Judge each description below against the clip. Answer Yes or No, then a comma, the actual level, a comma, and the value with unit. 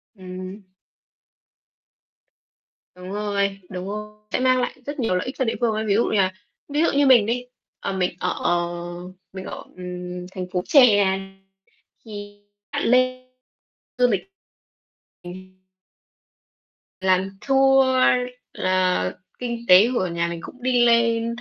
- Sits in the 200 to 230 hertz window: Yes, high, 205 Hz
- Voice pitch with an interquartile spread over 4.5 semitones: Yes, average, 4.9 semitones